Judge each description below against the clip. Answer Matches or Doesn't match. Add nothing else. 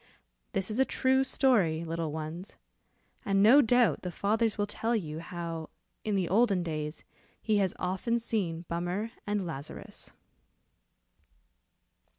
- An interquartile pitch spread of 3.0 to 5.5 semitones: Matches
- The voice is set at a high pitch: Matches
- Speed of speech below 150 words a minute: Matches